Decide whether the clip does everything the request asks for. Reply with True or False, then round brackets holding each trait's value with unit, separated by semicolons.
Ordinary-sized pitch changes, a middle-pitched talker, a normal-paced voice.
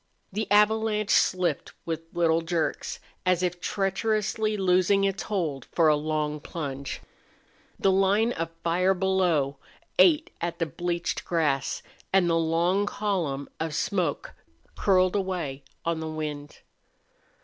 False (3.5 semitones; 175 Hz; 125 wpm)